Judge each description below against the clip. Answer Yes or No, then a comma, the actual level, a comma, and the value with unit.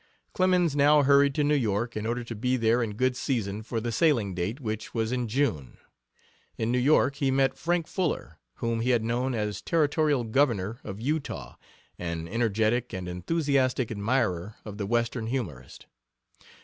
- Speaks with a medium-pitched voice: No, low, 120 Hz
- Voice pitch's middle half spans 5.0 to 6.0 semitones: No, average, 4.4 semitones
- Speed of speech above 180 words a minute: No, average, 170 wpm